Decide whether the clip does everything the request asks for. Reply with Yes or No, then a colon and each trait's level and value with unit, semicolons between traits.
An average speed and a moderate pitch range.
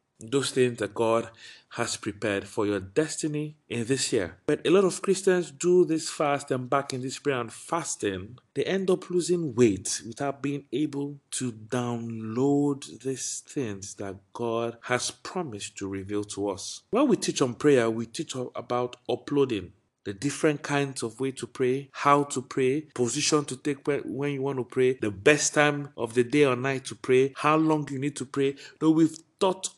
Yes: average, 185 wpm; average, 3.8 semitones